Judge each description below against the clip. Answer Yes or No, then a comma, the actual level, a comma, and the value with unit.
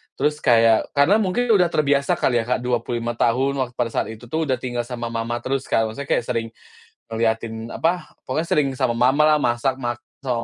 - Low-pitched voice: Yes, low, 125 Hz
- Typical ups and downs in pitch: Yes, average, 3.3 semitones